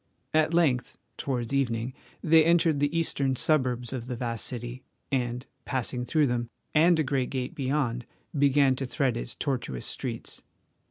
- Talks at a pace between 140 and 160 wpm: Yes, average, 155 wpm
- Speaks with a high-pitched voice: No, low, 130 Hz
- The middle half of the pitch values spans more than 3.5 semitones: No, average, 3.1 semitones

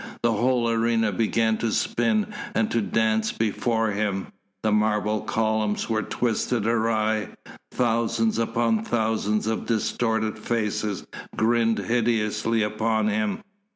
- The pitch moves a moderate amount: No, narrow, 1.2 semitones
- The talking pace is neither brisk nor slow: No, slow, 120 wpm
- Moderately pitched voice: No, low, 110 Hz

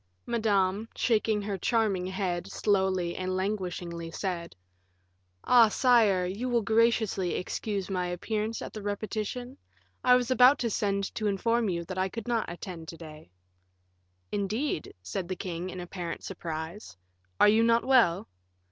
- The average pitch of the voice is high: Yes, high, 200 Hz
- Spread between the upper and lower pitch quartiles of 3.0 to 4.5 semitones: Yes, average, 3.9 semitones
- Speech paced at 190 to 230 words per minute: No, average, 145 wpm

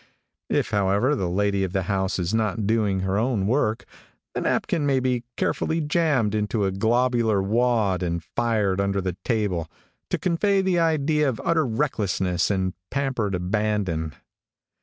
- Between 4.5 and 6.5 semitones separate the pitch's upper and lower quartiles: Yes, average, 5.0 semitones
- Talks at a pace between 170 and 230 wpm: No, average, 155 wpm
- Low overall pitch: Yes, low, 105 Hz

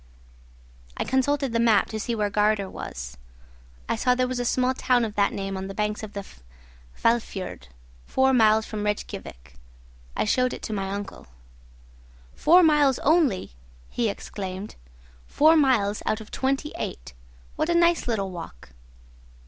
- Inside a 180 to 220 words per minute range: No, average, 155 wpm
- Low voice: No, high, 220 Hz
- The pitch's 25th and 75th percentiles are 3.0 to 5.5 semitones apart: Yes, average, 4.6 semitones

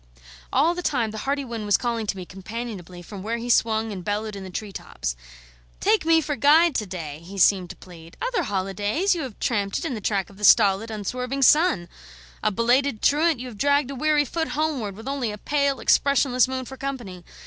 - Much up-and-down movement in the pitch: Yes, wide, 5.8 semitones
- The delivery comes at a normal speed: No, fast, 215 wpm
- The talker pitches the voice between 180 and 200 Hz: No, high, 230 Hz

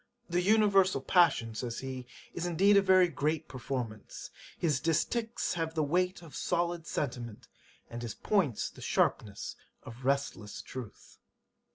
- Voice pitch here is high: No, medium, 155 Hz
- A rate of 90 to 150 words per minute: Yes, average, 140 wpm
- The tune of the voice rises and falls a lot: Yes, wide, 6.1 semitones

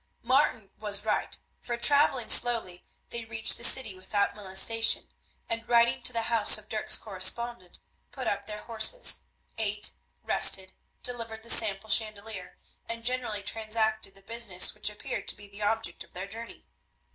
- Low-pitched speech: No, high, 220 Hz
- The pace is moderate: Yes, average, 155 wpm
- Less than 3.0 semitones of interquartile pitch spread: Yes, narrow, 2.5 semitones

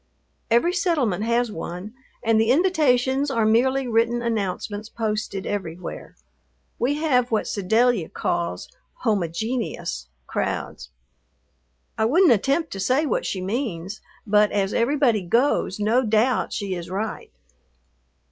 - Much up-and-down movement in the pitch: No, average, 4.3 semitones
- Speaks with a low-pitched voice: No, high, 225 Hz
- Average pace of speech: No, slow, 120 wpm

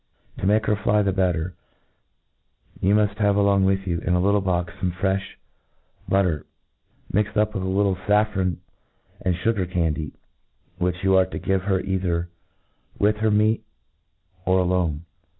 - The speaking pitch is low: Yes, very low, 95 Hz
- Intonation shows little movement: Yes, narrow, 2.3 semitones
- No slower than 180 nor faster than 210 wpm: No, average, 165 wpm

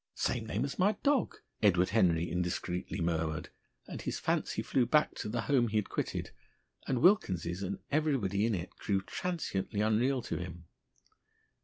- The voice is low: Yes, low, 105 Hz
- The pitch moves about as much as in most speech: No, wide, 6.7 semitones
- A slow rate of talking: No, average, 160 wpm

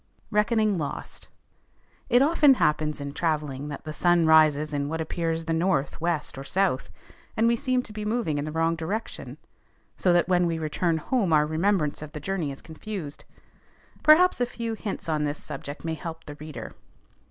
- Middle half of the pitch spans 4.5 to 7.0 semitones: Yes, average, 5.3 semitones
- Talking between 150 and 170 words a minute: No, average, 185 wpm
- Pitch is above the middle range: No, medium, 165 Hz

